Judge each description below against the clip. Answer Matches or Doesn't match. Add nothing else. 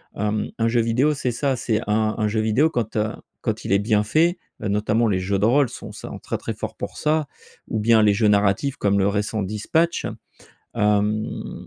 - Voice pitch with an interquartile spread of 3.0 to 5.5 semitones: Doesn't match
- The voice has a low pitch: Matches